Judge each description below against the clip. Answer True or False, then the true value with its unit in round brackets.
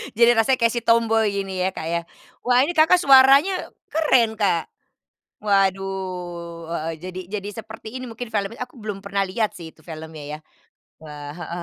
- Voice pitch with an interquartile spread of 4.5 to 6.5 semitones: True (5.1 semitones)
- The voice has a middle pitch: False (200 Hz)